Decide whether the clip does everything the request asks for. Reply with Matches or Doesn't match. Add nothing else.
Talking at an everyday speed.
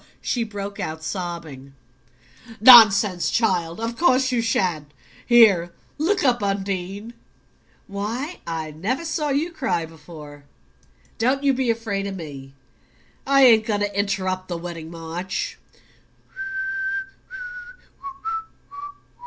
Doesn't match